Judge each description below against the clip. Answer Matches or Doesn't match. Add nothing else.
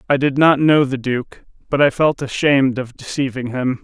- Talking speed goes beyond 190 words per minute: Matches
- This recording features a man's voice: Matches